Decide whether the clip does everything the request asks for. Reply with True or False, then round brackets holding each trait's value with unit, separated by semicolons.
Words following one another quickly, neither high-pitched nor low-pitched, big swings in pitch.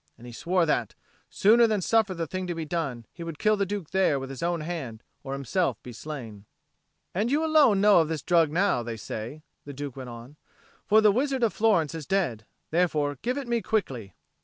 True (215 wpm; 165 Hz; 7.0 semitones)